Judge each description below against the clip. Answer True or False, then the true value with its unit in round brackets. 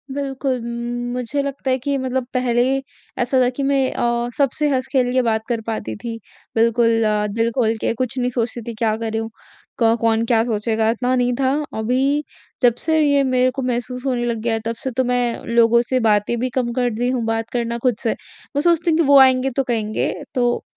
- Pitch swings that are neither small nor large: False (2.2 semitones)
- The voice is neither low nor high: False (245 Hz)